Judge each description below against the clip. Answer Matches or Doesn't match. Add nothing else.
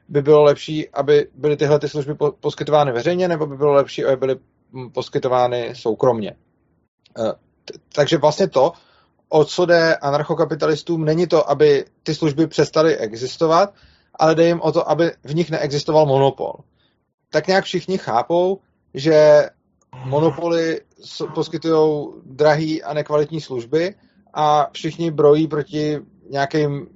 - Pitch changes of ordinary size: Doesn't match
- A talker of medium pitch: Matches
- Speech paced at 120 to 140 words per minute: Matches